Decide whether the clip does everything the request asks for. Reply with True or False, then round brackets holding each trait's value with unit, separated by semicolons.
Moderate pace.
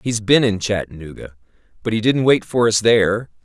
True (190 wpm)